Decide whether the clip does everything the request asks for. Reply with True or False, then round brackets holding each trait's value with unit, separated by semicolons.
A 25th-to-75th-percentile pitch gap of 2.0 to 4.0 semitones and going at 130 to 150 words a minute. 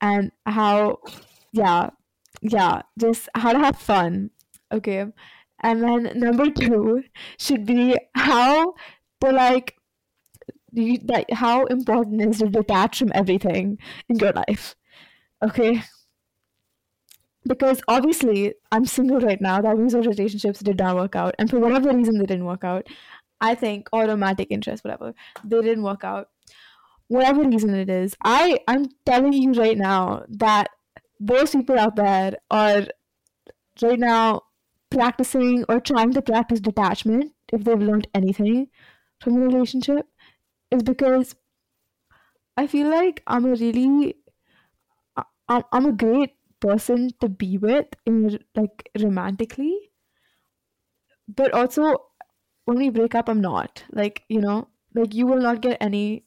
True (3.3 semitones; 135 wpm)